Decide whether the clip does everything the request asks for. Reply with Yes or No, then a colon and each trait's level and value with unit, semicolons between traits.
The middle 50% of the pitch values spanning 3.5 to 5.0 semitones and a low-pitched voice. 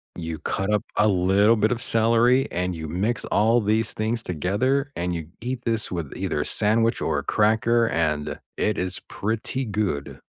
Yes: average, 4.3 semitones; low, 105 Hz